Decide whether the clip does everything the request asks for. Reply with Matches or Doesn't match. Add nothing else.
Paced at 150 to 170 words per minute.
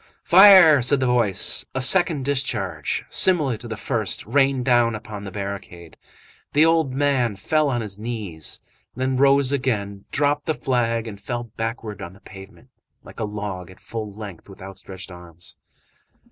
Matches